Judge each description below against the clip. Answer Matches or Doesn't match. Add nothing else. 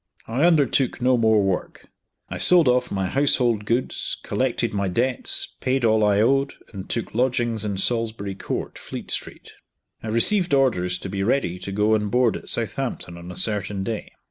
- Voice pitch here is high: Doesn't match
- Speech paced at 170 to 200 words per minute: Matches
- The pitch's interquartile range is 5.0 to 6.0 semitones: Doesn't match